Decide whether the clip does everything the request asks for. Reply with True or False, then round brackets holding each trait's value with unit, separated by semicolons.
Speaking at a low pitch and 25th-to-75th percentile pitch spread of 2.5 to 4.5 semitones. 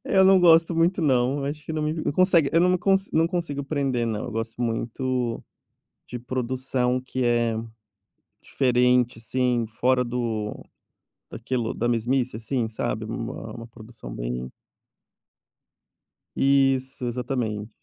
True (125 Hz; 3.2 semitones)